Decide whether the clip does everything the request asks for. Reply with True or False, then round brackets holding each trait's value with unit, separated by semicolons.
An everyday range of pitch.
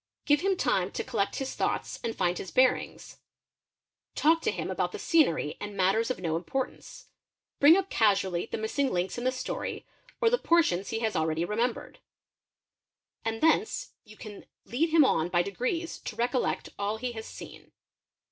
False (6.7 semitones)